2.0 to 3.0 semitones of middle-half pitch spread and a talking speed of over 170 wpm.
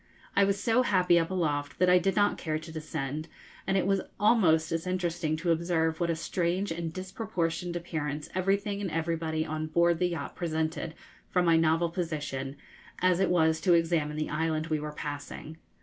Yes: narrow, 2.4 semitones; average, 185 wpm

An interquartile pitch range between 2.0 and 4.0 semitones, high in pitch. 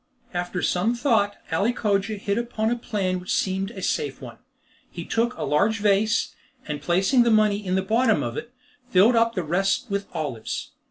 Yes: average, 3.7 semitones; high, 200 Hz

